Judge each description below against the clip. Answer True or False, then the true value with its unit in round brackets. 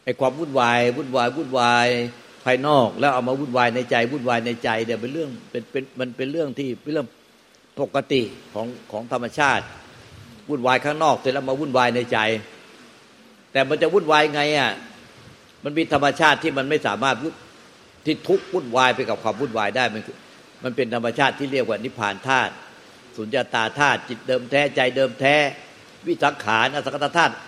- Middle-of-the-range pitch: False (130 Hz)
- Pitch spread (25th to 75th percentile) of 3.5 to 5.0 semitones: False (3.1 semitones)